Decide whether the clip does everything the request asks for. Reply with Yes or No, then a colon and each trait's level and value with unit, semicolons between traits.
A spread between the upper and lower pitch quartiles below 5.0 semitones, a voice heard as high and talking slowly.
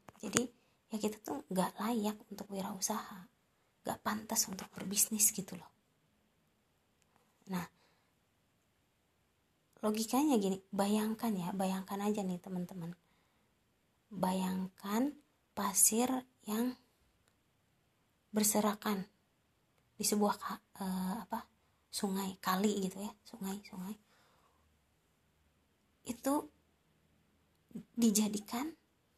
Yes: average, 2.8 semitones; high, 205 Hz; slow, 80 wpm